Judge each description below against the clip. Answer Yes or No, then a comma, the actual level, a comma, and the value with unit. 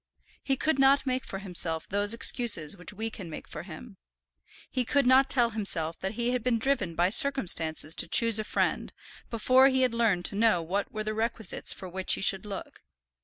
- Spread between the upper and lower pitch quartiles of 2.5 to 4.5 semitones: No, average, 5.1 semitones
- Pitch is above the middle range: Yes, high, 215 Hz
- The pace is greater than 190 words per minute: Yes, fast, 205 wpm